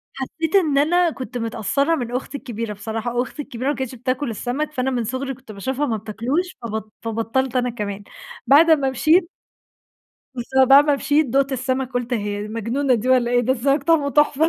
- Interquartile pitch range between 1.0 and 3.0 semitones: No, average, 3.5 semitones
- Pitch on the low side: No, very high, 260 Hz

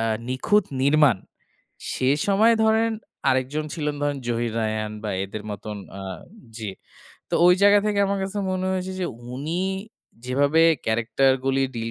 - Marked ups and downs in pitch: Yes, wide, 8.1 semitones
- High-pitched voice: No, medium, 140 Hz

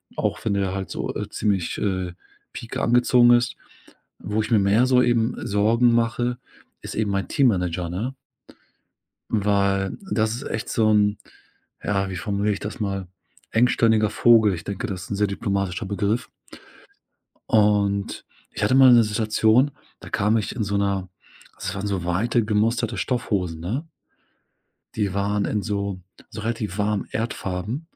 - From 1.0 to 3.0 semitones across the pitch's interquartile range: Yes, average, 2.7 semitones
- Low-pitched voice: Yes, low, 105 Hz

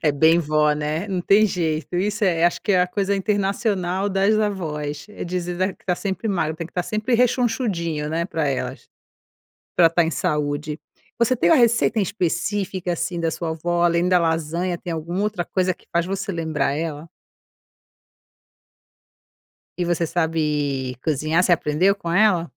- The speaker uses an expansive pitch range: No, average, 3.4 semitones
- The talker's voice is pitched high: No, medium, 175 Hz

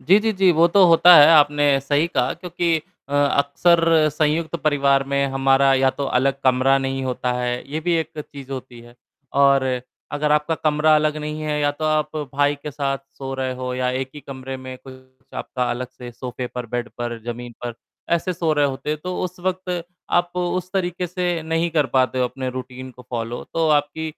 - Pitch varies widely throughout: No, average, 3.7 semitones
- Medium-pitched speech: Yes, medium, 145 Hz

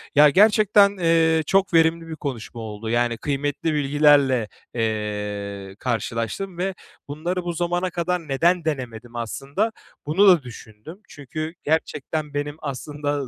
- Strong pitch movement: Yes, wide, 5.9 semitones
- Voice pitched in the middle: Yes, medium, 145 Hz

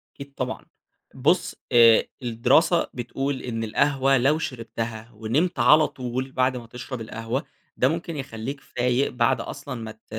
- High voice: No, low, 125 Hz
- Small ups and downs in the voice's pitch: No, average, 3.1 semitones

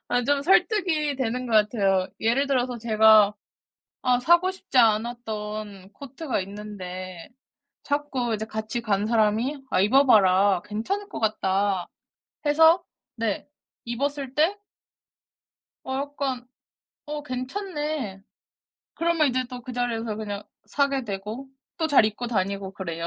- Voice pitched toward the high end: Yes, high, 240 Hz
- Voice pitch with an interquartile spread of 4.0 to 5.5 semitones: Yes, average, 5.1 semitones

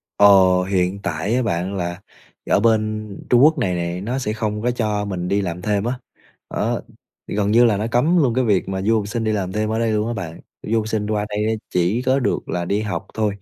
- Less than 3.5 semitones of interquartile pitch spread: Yes, average, 2.9 semitones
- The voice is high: No, low, 105 Hz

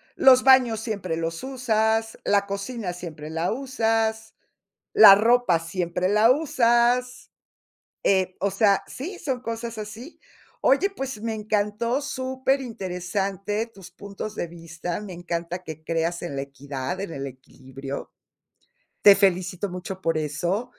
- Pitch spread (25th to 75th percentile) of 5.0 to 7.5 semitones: Yes, average, 5.3 semitones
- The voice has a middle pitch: No, high, 200 Hz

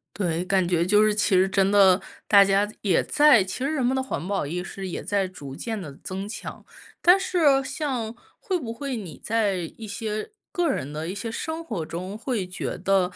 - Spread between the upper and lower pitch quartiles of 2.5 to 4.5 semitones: No, average, 5.0 semitones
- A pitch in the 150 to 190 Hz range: No, high, 205 Hz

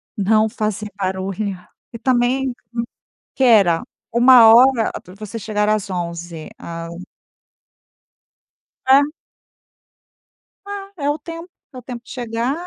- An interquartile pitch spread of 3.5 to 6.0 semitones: Yes, average, 4.7 semitones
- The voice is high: Yes, high, 225 Hz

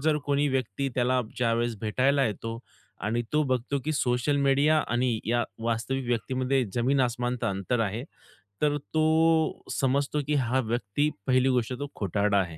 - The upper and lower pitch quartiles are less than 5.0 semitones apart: Yes, average, 3.2 semitones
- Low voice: Yes, low, 130 Hz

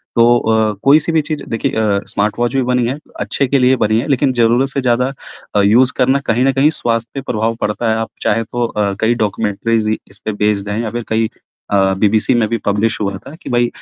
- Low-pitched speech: Yes, low, 115 Hz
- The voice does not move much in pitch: No, average, 3.0 semitones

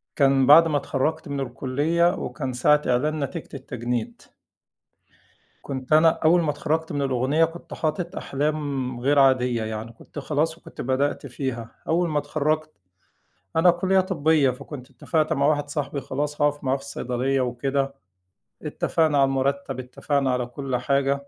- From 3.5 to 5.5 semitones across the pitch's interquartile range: No, average, 2.9 semitones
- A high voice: No, medium, 140 Hz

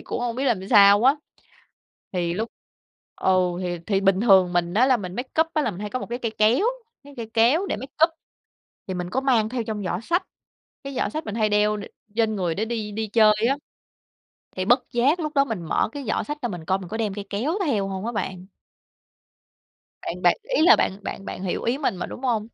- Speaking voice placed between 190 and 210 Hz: No, high, 220 Hz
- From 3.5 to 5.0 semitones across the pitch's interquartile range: Yes, average, 4.7 semitones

